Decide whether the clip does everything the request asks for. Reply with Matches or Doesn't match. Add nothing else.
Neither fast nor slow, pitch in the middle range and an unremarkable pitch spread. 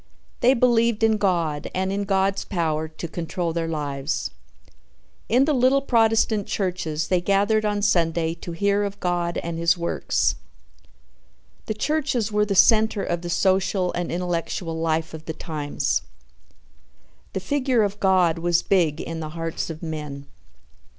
Matches